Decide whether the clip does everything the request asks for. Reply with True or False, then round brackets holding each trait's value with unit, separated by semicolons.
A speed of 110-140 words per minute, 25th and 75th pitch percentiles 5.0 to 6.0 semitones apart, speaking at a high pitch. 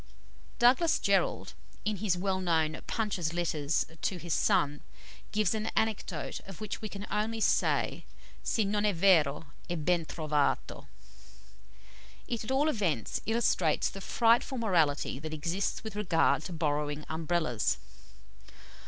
False (135 wpm; 5.4 semitones; 180 Hz)